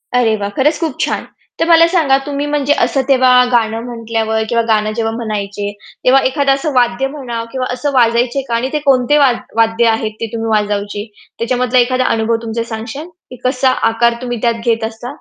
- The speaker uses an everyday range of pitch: Yes, average, 3.0 semitones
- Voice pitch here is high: Yes, high, 240 Hz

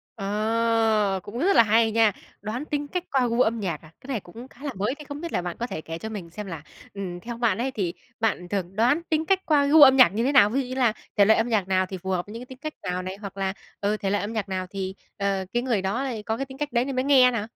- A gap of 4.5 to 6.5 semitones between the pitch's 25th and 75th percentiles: Yes, average, 4.8 semitones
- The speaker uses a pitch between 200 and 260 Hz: Yes, high, 225 Hz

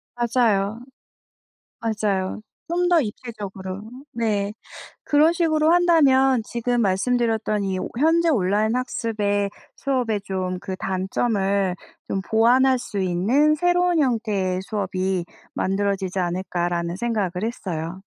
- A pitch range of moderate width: Yes, average, 4.9 semitones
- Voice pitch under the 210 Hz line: No, high, 215 Hz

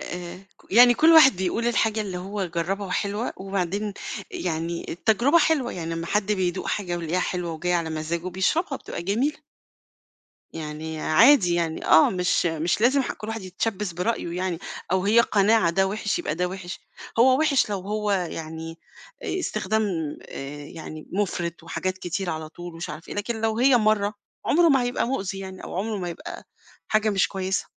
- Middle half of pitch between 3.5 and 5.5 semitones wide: Yes, average, 4.2 semitones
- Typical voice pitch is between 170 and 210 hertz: Yes, high, 190 Hz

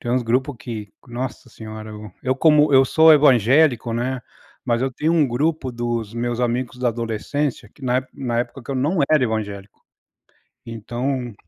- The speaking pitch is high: No, low, 125 Hz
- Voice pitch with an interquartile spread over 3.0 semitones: No, average, 2.7 semitones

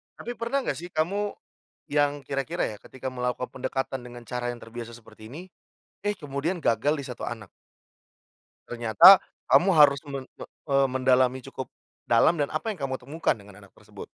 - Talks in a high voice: No, low, 135 Hz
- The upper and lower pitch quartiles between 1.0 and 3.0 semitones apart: No, average, 4.0 semitones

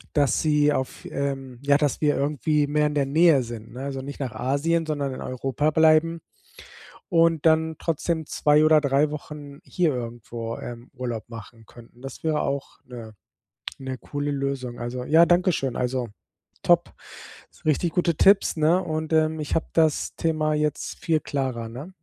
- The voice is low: No, medium, 145 Hz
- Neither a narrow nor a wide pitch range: Yes, average, 3.5 semitones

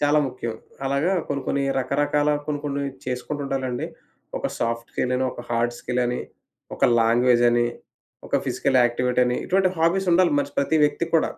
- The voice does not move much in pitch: No, average, 3.1 semitones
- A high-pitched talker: No, low, 135 Hz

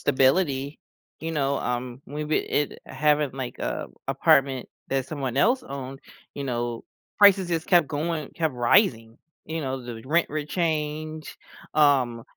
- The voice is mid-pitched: Yes, medium, 145 Hz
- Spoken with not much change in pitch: No, average, 3.1 semitones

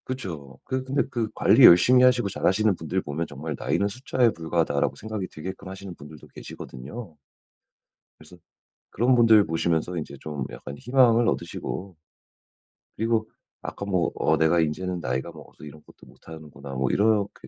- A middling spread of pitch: No, wide, 6.0 semitones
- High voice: No, very low, 90 Hz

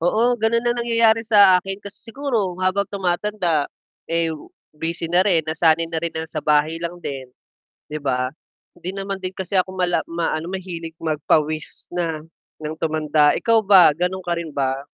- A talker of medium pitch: Yes, medium, 175 Hz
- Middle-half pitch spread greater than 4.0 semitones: No, average, 3.6 semitones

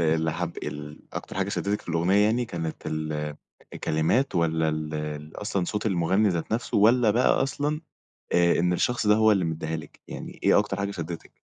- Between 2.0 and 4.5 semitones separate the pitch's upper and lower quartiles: No, average, 4.9 semitones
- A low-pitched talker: Yes, very low, 85 Hz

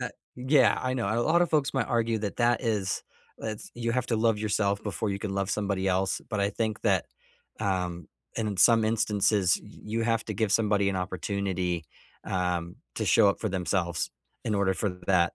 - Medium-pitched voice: No, low, 105 Hz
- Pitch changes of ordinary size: Yes, average, 3.0 semitones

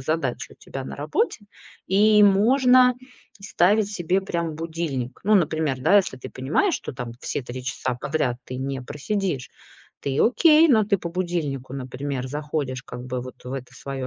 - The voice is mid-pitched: Yes, medium, 150 Hz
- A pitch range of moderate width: No, wide, 7.2 semitones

